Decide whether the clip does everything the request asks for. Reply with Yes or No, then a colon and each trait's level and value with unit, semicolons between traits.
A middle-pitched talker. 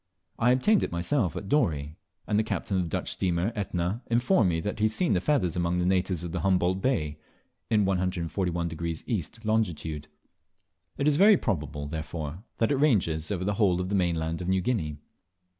No: very low, 90 Hz